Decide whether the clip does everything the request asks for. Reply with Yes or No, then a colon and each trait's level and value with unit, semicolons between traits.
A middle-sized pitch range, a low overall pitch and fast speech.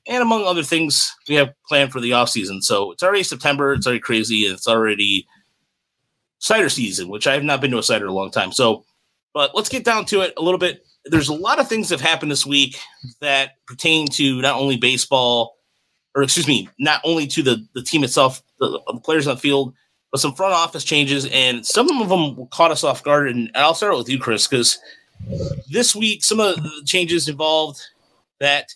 No: average, 4.4 semitones; medium, 145 Hz; fast, 215 wpm